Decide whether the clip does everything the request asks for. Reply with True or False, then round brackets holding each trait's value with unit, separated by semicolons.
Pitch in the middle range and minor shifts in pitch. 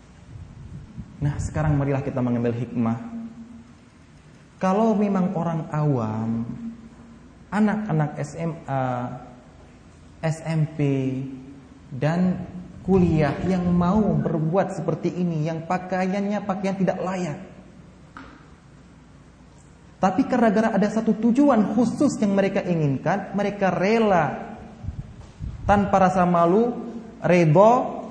False (180 Hz; 5.1 semitones)